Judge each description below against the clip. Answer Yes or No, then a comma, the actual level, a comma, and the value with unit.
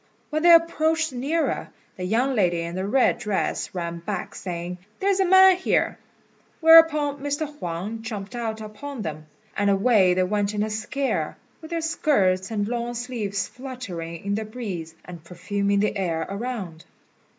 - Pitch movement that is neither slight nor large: No, wide, 7.0 semitones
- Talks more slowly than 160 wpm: No, average, 165 wpm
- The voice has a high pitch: Yes, high, 215 Hz